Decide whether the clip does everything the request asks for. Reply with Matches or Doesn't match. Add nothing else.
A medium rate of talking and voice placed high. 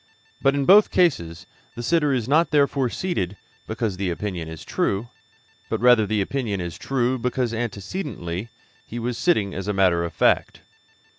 Doesn't match